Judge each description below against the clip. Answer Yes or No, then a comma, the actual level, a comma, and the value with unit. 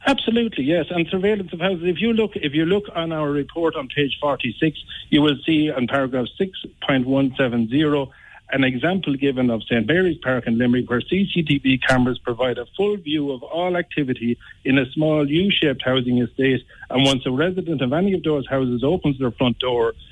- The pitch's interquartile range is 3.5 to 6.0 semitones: Yes, average, 5.0 semitones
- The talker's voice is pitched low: No, medium, 145 Hz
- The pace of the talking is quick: No, average, 190 wpm